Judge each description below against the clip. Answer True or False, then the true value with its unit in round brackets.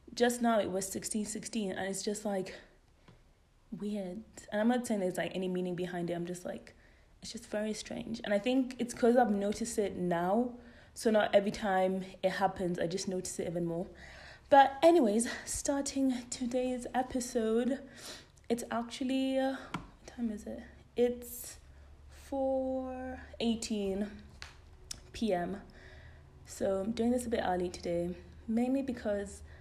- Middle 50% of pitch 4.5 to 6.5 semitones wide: True (4.8 semitones)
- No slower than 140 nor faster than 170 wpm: True (150 wpm)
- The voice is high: True (215 Hz)